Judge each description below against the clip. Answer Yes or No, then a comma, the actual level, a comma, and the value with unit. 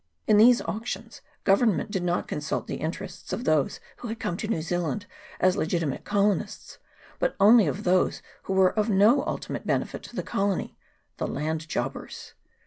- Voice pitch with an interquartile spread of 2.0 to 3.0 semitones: No, average, 3.7 semitones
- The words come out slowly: No, average, 170 wpm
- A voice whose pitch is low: No, high, 195 Hz